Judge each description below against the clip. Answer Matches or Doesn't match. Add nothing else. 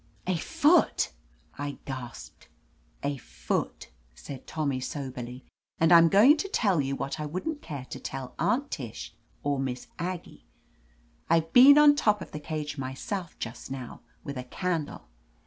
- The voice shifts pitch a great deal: Matches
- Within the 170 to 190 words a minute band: Doesn't match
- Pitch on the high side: Doesn't match